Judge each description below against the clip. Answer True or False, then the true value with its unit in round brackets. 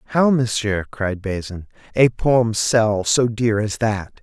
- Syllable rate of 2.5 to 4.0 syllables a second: True (3.6 syllables/s)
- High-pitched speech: False (110 Hz)